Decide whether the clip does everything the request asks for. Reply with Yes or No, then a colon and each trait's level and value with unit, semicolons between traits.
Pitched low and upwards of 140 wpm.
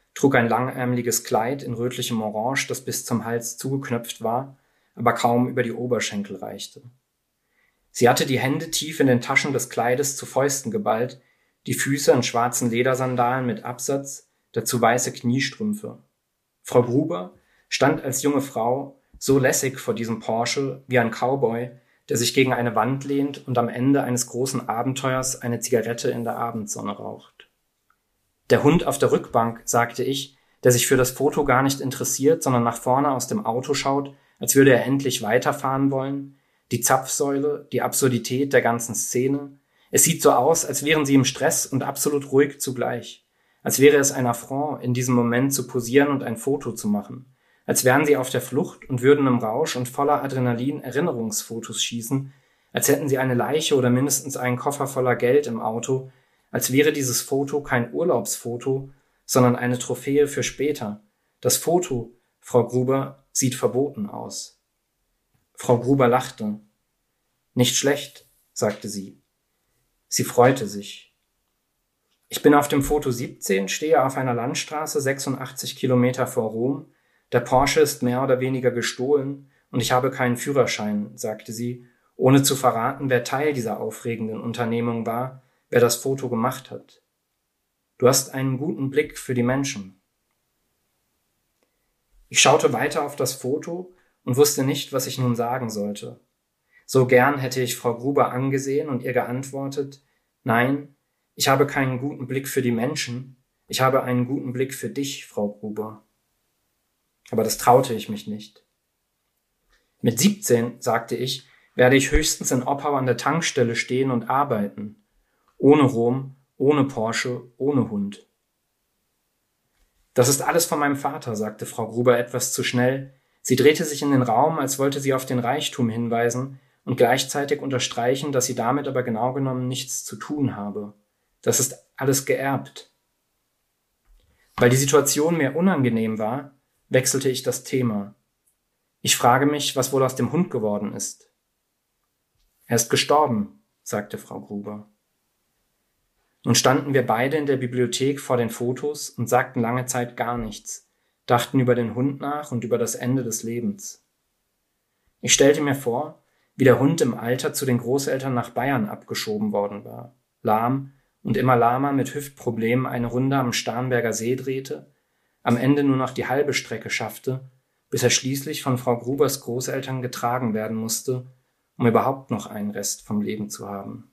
Yes: low, 130 Hz; average, 160 wpm